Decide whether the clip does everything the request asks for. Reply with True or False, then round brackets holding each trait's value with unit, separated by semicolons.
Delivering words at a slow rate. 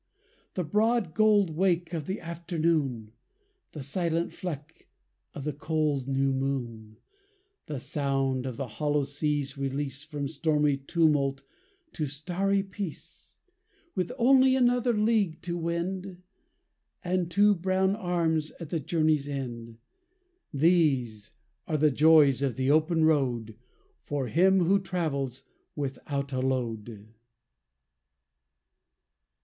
True (115 wpm)